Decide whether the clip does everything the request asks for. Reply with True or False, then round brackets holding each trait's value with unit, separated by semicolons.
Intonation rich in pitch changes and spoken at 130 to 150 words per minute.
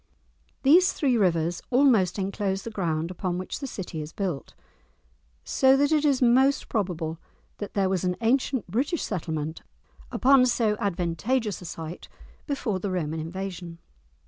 True (6.6 semitones; 145 wpm)